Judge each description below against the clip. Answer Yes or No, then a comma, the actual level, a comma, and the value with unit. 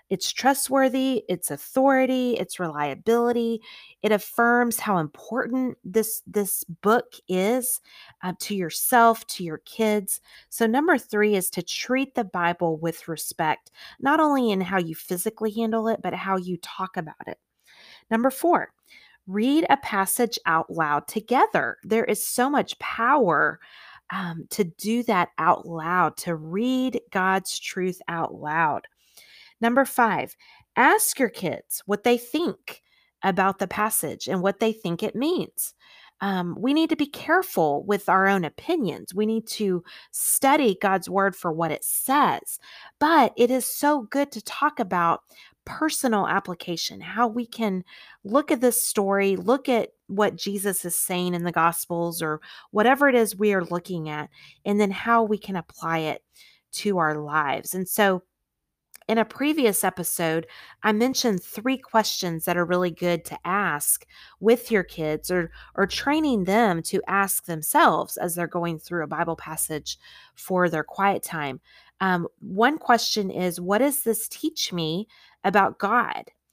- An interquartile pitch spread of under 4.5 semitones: No, average, 5.2 semitones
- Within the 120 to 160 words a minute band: Yes, average, 155 wpm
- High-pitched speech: Yes, high, 205 Hz